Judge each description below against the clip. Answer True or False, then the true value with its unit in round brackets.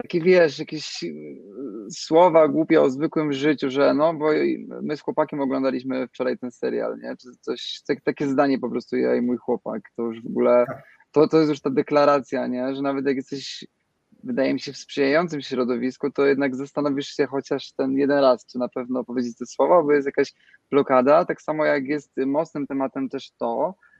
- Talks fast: True (195 wpm)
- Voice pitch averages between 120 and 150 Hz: True (140 Hz)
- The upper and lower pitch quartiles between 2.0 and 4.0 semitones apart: True (2.7 semitones)